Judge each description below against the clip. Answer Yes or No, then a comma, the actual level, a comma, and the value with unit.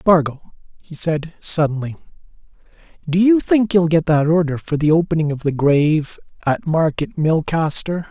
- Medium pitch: Yes, medium, 160 Hz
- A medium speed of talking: Yes, average, 150 wpm